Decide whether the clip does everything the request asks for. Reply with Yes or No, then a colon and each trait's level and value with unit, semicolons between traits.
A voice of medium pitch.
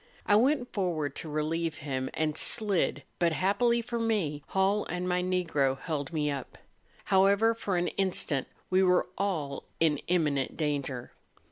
Yes: medium, 175 Hz